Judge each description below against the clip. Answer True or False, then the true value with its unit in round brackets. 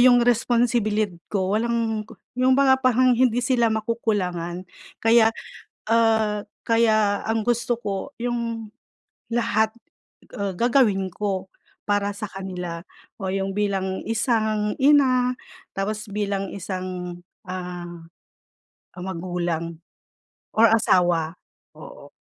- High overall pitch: True (215 Hz)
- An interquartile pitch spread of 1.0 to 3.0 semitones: False (3.6 semitones)